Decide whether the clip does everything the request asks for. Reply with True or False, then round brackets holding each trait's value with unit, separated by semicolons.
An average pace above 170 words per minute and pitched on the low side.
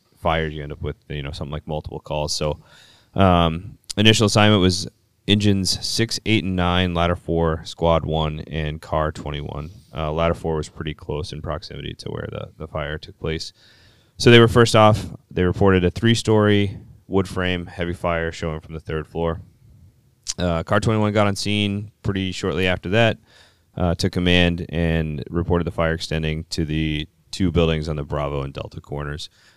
True (180 wpm; 85 Hz)